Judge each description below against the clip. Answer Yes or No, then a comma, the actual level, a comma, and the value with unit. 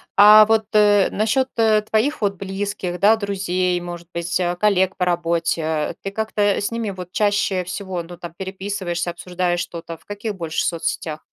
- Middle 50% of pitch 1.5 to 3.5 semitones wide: Yes, average, 3.0 semitones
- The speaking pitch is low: No, high, 190 Hz